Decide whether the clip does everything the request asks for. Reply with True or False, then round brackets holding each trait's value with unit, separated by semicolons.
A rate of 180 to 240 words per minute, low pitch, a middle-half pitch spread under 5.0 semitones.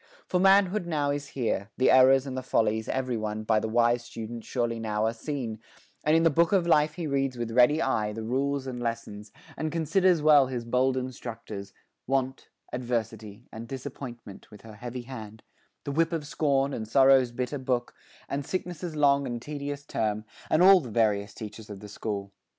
True (185 wpm; 130 Hz; 4.3 semitones)